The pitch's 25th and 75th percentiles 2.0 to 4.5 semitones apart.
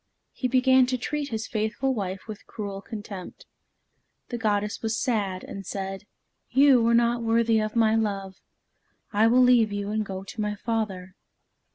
Yes: average, 2.7 semitones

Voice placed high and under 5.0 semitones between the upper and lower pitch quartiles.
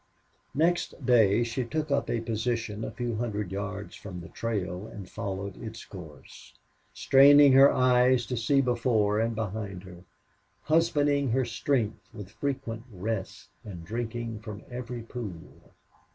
No: low, 115 Hz; average, 3.7 semitones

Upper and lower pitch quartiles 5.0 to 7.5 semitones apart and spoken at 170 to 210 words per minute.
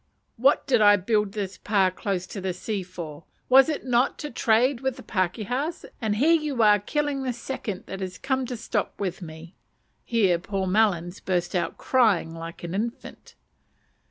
Yes: wide, 5.4 semitones; average, 180 wpm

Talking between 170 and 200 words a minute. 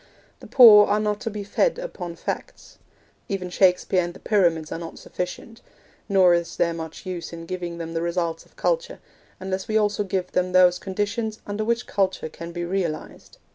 Yes: average, 185 wpm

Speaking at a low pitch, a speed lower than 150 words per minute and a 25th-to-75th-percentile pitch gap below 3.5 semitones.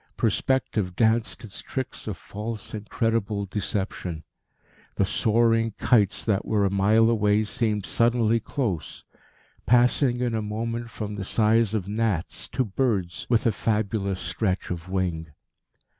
Yes: low, 110 Hz; slow, 135 wpm; average, 2.7 semitones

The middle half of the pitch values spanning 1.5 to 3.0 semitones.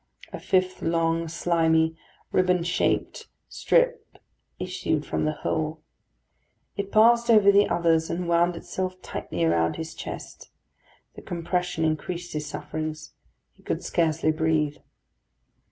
Yes: narrow, 2.6 semitones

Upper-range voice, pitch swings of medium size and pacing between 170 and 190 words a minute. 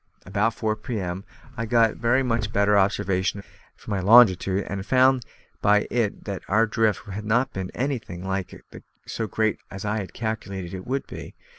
No: low, 105 Hz; average, 3.0 semitones; average, 180 wpm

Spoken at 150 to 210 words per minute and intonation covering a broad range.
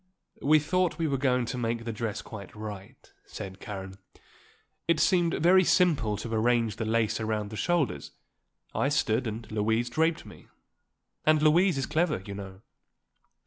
Yes: average, 160 wpm; wide, 6.4 semitones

